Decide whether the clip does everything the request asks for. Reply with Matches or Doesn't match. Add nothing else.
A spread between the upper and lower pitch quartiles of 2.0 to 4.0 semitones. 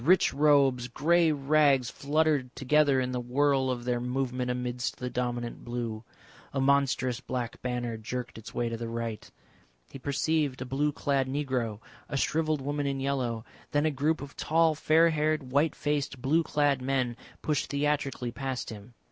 Matches